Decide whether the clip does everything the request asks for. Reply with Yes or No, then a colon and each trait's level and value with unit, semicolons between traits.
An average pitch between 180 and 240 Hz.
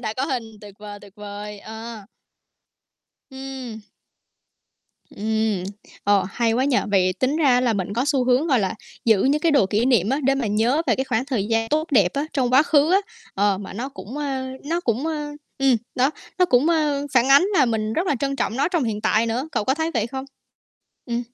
No: very high, 250 Hz